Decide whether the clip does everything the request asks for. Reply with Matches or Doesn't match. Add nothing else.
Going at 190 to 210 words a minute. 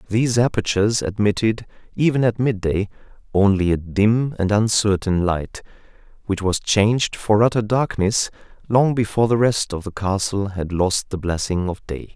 Doesn't match